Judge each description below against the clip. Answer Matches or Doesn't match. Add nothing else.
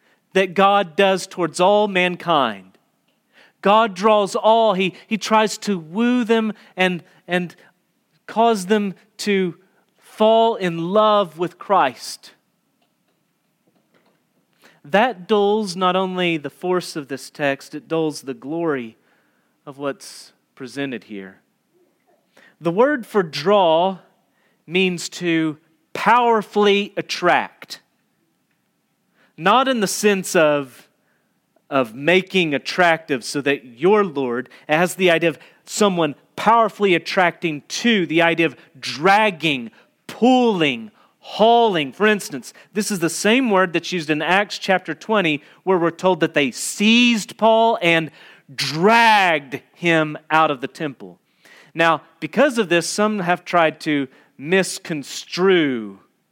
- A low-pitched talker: Doesn't match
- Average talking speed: Doesn't match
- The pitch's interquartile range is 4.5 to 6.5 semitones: Matches